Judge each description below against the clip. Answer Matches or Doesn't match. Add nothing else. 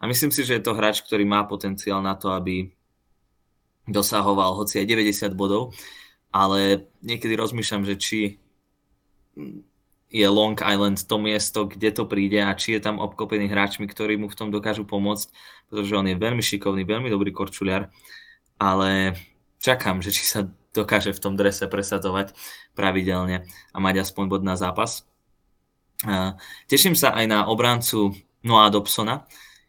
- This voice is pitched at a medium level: Doesn't match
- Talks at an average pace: Matches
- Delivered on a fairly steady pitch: Matches